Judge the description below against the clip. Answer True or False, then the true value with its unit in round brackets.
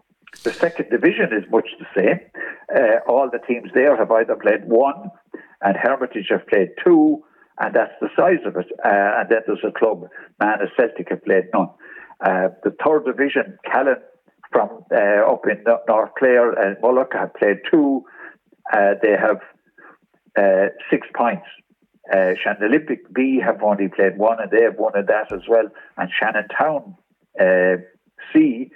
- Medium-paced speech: True (170 wpm)